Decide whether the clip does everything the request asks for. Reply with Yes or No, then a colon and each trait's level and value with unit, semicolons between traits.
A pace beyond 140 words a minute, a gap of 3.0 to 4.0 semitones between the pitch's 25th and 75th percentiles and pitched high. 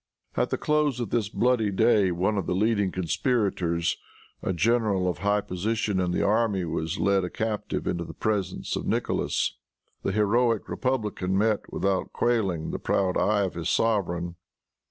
No: average, 165 wpm; average, 3.5 semitones; low, 100 Hz